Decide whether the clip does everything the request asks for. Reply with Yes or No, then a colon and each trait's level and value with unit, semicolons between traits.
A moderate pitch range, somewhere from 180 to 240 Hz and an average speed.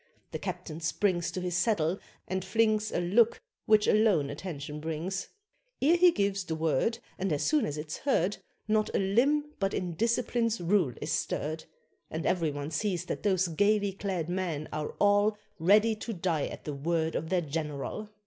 Yes: average, 4.9 semitones; medium, 185 Hz; average, 175 wpm